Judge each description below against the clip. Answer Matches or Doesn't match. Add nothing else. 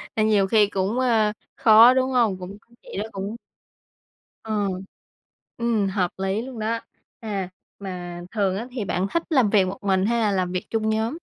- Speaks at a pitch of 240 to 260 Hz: Doesn't match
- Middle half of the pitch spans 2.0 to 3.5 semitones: Matches